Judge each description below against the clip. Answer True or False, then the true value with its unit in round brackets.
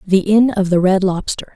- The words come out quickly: True (230 wpm)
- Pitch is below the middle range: False (195 Hz)